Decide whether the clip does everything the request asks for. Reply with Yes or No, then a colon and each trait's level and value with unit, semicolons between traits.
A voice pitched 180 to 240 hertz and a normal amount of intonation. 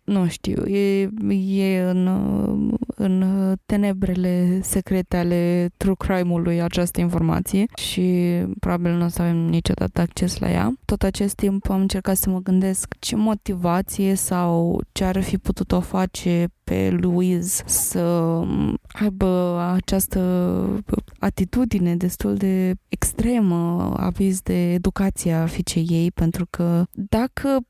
No: medium, 185 Hz; narrow, 2.0 semitones